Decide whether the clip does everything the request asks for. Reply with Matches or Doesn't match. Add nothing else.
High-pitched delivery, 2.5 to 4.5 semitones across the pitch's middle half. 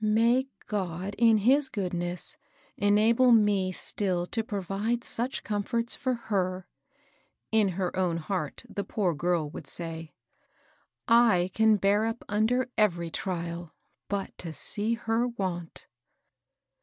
Matches